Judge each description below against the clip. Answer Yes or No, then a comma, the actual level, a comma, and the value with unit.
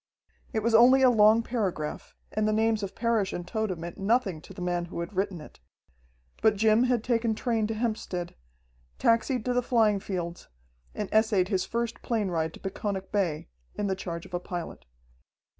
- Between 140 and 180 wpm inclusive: No, average, 190 wpm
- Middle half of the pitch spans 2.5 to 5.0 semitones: Yes, average, 4.0 semitones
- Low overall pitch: No, high, 210 Hz